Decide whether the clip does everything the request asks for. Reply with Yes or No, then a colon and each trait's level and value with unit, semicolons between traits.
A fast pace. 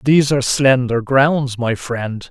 No: average, 155 wpm